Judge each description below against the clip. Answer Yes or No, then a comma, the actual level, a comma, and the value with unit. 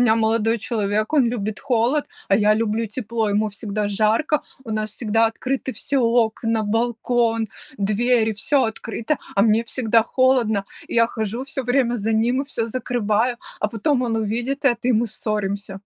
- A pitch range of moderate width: No, narrow, 2.3 semitones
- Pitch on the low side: No, high, 225 Hz